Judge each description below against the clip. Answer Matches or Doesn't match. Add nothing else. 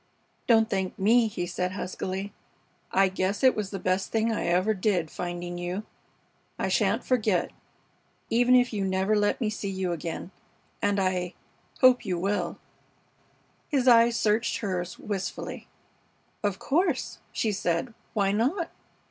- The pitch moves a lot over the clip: Doesn't match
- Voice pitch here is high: Matches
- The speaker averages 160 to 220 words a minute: Doesn't match